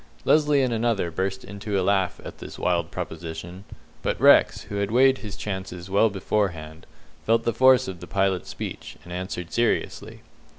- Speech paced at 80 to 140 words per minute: No, average, 170 wpm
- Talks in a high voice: No, low, 100 Hz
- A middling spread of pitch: Yes, average, 4.2 semitones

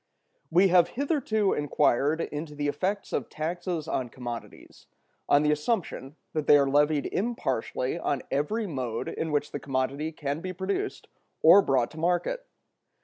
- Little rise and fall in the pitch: No, average, 4.4 semitones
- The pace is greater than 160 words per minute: No, average, 150 wpm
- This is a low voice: No, medium, 155 Hz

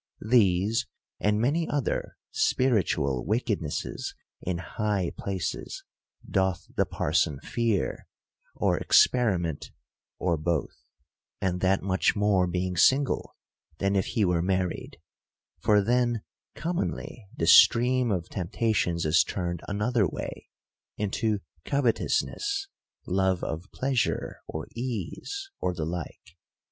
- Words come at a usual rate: No, slow, 110 wpm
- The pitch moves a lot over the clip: No, average, 5.0 semitones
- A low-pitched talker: Yes, low, 100 Hz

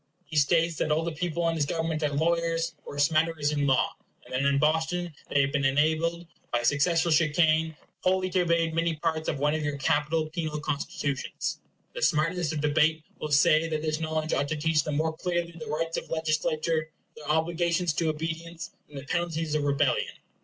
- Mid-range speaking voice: Yes, medium, 160 Hz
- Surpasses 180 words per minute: Yes, average, 195 wpm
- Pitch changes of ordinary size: No, narrow, 1.8 semitones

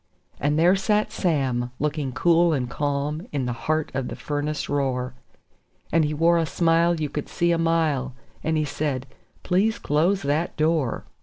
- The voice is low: No, medium, 150 Hz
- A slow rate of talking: No, average, 170 wpm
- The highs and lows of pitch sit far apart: No, average, 3.0 semitones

